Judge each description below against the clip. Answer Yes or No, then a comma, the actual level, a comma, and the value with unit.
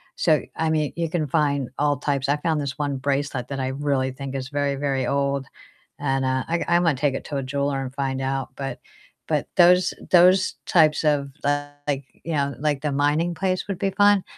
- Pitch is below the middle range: No, medium, 145 Hz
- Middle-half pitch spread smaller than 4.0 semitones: Yes, narrow, 2.5 semitones